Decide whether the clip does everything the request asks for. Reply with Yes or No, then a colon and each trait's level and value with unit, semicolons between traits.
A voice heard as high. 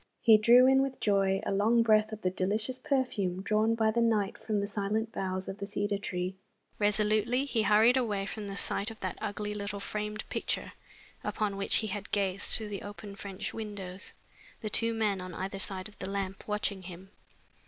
Yes: high, 205 Hz